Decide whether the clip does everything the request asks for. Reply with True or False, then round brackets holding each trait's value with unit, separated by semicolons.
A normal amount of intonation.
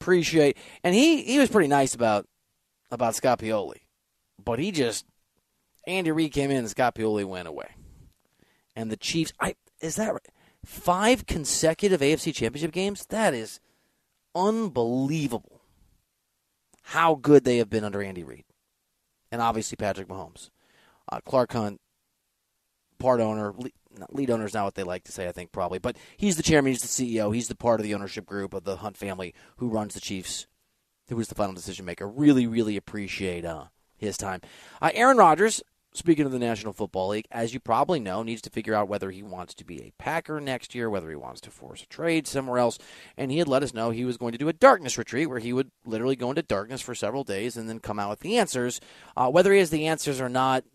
False (7.0 semitones)